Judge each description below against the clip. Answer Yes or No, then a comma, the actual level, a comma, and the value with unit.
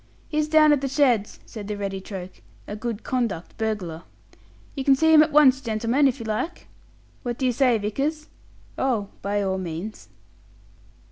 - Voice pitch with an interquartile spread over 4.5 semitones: Yes, average, 5.2 semitones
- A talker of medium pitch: No, high, 235 Hz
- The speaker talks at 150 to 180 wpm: Yes, average, 175 wpm